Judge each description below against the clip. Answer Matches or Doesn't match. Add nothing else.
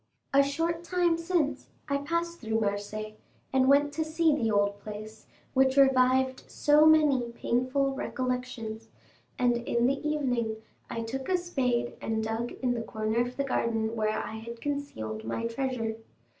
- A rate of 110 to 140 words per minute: Doesn't match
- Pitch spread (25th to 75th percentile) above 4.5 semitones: Doesn't match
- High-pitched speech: Matches